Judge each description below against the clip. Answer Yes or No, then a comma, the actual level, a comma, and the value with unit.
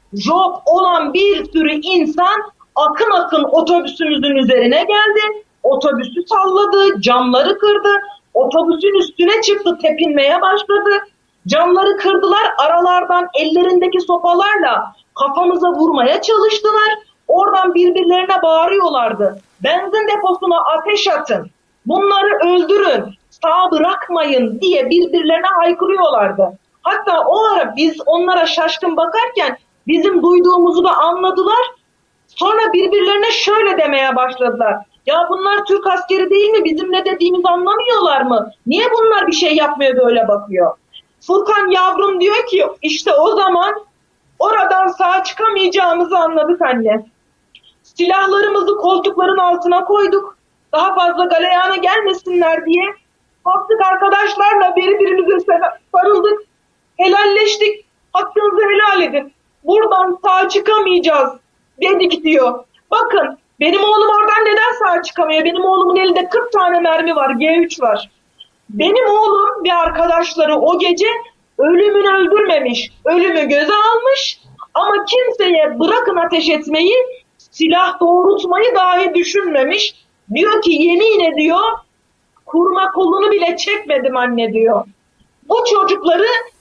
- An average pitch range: Yes, average, 3.6 semitones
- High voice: Yes, very high, 365 Hz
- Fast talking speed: No, average, 110 wpm